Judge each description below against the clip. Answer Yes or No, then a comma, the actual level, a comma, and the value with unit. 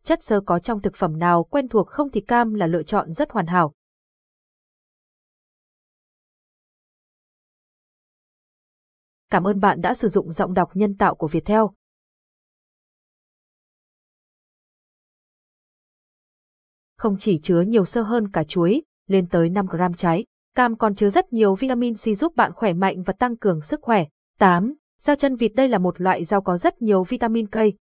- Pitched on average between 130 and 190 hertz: No, high, 205 Hz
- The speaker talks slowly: Yes, slow, 155 wpm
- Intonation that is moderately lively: Yes, average, 4.4 semitones